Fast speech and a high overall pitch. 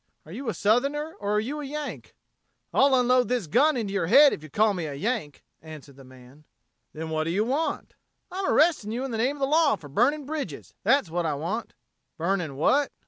Yes: fast, 220 wpm; high, 220 Hz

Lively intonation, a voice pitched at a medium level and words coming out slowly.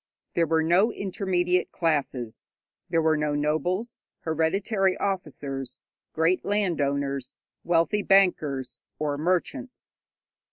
No: average, 4.5 semitones; medium, 165 Hz; slow, 95 wpm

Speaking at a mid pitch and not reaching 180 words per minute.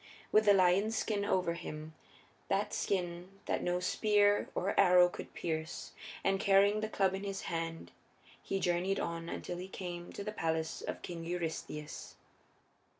Yes: medium, 180 Hz; average, 155 wpm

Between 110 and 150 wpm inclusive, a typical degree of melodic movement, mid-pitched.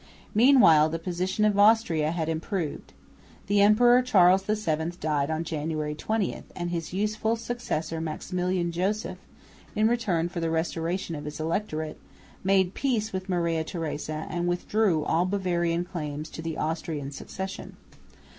Yes: average, 140 wpm; average, 4.1 semitones; medium, 175 Hz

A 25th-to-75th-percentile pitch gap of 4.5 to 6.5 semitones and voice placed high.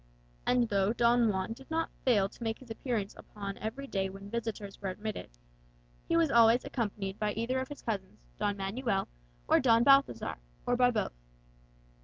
No: average, 3.7 semitones; high, 225 Hz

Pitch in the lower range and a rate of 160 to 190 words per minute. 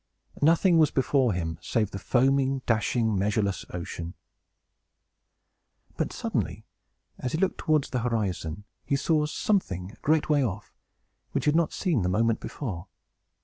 No: low, 120 Hz; average, 145 wpm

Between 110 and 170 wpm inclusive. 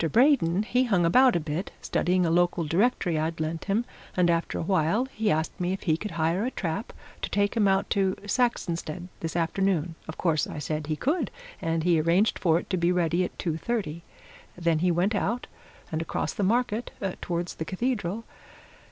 No: average, 195 wpm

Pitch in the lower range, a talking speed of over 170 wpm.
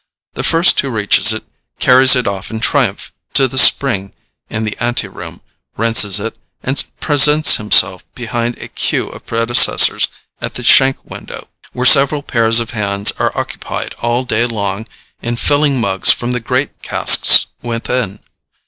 No: low, 120 Hz; average, 155 wpm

